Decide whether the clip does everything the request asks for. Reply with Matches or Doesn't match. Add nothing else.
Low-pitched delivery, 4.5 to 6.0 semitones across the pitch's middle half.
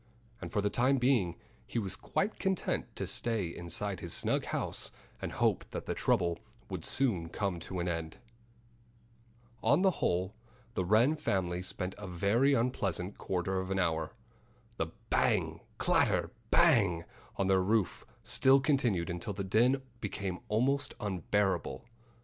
Matches